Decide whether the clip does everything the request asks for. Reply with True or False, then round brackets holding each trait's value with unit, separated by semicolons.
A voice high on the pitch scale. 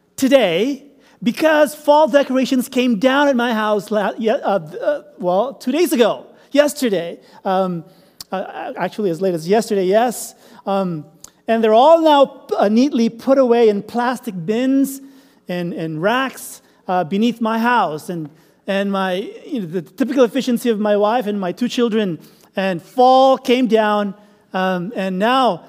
True (230 Hz)